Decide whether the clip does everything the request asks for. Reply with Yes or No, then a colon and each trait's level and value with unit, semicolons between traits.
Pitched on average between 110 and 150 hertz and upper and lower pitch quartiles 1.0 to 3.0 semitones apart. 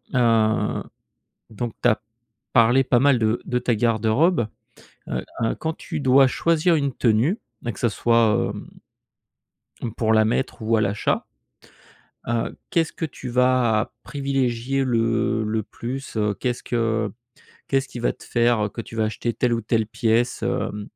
Yes: low, 120 Hz; narrow, 2.5 semitones